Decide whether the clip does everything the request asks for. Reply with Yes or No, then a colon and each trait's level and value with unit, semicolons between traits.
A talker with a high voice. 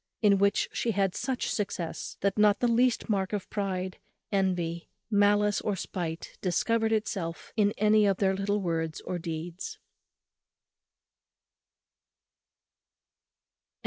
Yes: high, 200 Hz